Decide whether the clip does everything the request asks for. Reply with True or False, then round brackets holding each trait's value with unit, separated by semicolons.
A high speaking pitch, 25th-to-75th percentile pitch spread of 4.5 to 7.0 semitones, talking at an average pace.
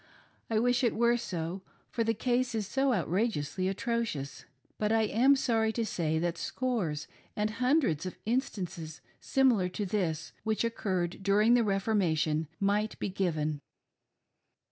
True (210 Hz; 5.2 semitones; 145 wpm)